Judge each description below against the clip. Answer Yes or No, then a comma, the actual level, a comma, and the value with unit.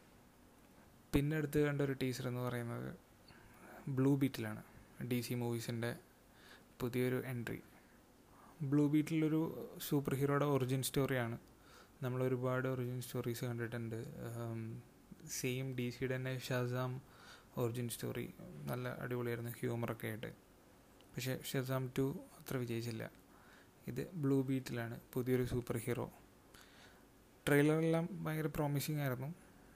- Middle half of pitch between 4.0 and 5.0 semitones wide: No, average, 2.8 semitones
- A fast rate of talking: No, average, 100 wpm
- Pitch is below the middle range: Yes, low, 130 Hz